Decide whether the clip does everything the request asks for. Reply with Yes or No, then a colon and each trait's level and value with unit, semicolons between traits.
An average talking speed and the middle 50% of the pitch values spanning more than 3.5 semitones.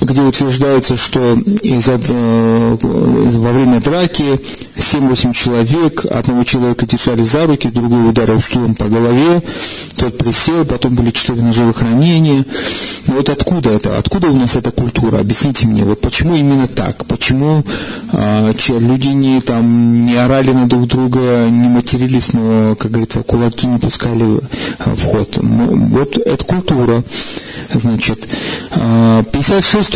No: average, 135 wpm; narrow, 2.5 semitones